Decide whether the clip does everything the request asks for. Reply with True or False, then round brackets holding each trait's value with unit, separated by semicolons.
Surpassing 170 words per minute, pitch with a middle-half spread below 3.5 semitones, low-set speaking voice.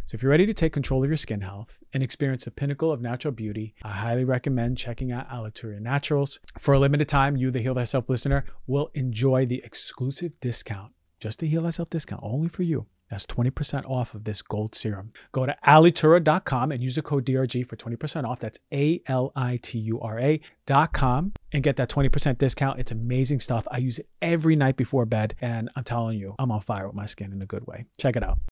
False (205 wpm; 3.8 semitones; 130 Hz)